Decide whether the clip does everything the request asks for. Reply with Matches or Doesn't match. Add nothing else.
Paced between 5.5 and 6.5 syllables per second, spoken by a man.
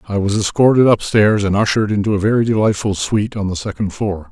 Matches